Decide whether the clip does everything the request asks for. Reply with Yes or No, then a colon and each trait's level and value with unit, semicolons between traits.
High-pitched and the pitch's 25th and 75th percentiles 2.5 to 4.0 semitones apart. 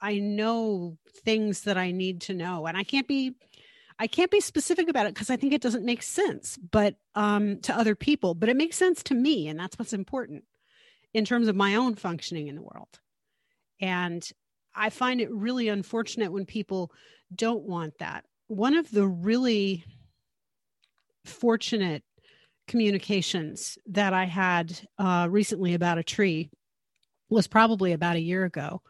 No: high, 210 Hz; average, 4.4 semitones